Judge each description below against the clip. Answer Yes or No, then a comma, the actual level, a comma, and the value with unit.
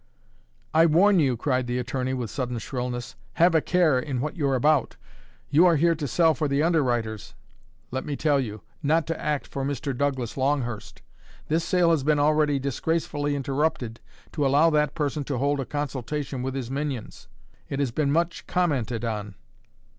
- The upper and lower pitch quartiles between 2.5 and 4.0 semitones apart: Yes, average, 3.3 semitones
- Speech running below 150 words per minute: No, average, 175 wpm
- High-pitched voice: No, medium, 140 Hz